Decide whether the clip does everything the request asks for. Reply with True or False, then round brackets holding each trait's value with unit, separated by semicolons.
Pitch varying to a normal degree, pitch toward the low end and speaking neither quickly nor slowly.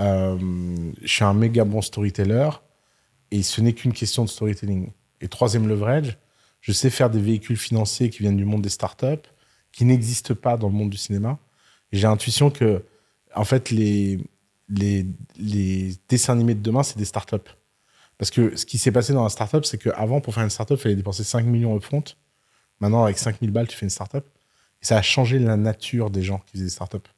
True (3.3 semitones; 110 Hz; 210 wpm)